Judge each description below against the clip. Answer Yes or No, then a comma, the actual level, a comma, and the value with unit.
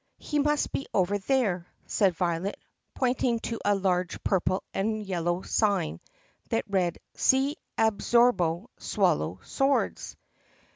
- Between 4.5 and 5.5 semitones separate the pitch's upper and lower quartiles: Yes, average, 5.2 semitones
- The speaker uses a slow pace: Yes, slow, 125 wpm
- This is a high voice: Yes, high, 200 Hz